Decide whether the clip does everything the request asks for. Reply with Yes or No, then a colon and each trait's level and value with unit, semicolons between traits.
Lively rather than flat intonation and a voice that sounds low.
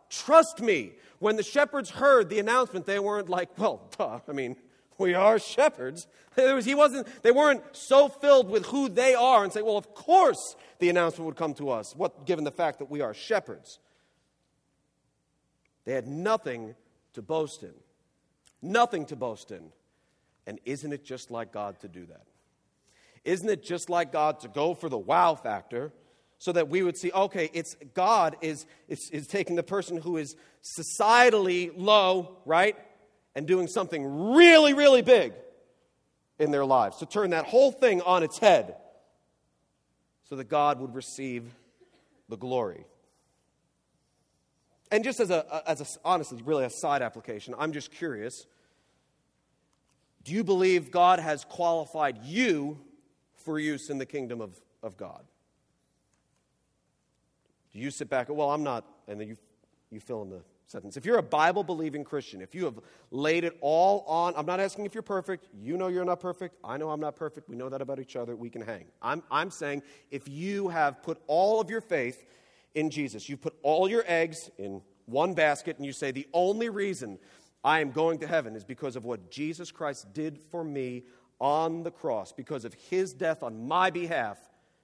No: wide, 5.9 semitones; medium, 160 Hz